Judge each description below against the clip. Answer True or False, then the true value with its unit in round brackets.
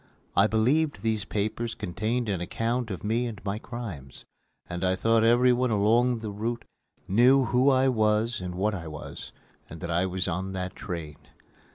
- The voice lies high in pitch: False (110 Hz)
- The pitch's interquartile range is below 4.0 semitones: False (4.3 semitones)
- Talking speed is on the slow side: False (175 wpm)